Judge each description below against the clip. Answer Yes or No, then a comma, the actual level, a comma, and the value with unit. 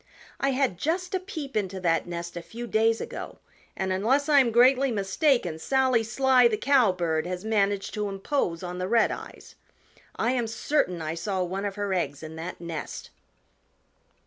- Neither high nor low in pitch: No, high, 210 Hz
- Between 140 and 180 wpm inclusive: Yes, average, 170 wpm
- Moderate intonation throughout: No, wide, 6.3 semitones